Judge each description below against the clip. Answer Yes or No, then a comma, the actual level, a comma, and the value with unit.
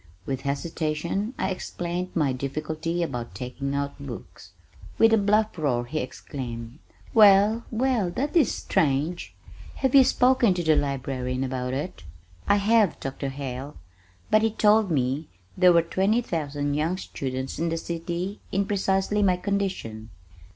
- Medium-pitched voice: Yes, medium, 165 Hz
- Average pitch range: No, wide, 6.5 semitones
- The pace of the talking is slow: No, average, 145 wpm